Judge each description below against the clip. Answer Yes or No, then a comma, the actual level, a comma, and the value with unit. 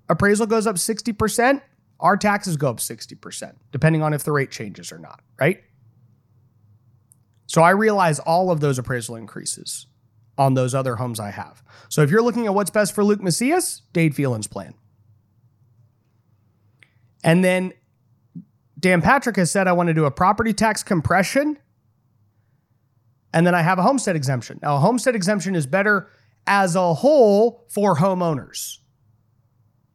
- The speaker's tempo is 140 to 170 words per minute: Yes, average, 155 wpm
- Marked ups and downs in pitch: Yes, wide, 8.5 semitones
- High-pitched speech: No, medium, 150 Hz